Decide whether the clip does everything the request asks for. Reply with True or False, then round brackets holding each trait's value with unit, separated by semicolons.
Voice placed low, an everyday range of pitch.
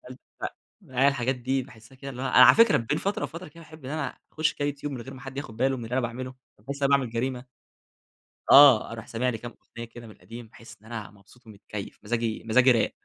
True (125 Hz; 3.1 semitones)